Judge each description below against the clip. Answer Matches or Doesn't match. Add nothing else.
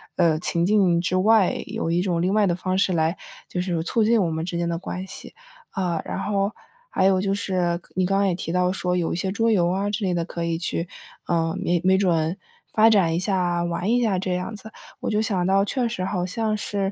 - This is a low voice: Doesn't match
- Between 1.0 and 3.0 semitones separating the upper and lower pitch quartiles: Matches